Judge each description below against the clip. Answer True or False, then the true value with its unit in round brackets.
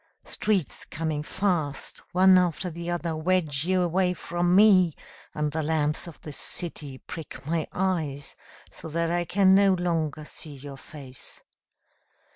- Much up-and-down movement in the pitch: False (3.2 semitones)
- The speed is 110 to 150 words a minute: True (145 wpm)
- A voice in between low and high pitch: True (165 Hz)